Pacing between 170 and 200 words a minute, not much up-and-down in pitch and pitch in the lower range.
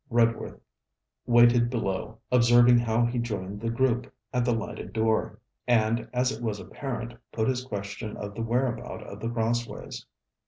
No: average, 155 wpm; narrow, 1.5 semitones; low, 120 Hz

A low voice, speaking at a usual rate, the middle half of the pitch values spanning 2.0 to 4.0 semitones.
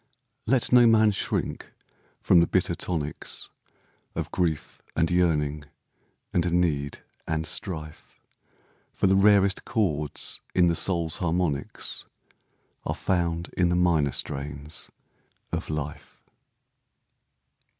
No: very low, 85 Hz; slow, 110 wpm; average, 3.1 semitones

